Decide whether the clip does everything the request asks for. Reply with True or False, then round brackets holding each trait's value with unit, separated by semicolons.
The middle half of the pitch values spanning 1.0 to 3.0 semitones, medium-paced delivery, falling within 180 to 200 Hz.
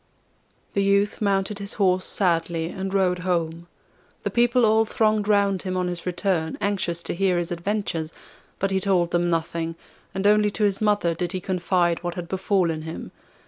True (2.7 semitones; 180 wpm; 185 Hz)